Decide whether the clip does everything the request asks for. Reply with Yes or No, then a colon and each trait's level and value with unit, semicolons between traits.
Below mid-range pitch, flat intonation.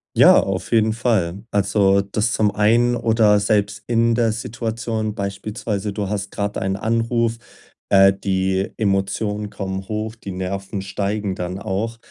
Yes: low, 105 Hz; narrow, 2.3 semitones